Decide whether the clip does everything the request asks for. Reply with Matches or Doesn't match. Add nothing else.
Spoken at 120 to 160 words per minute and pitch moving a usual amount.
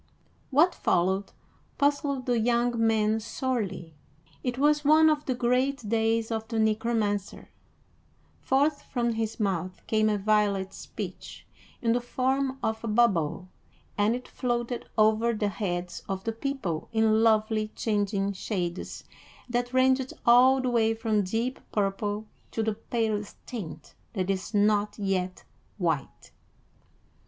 Matches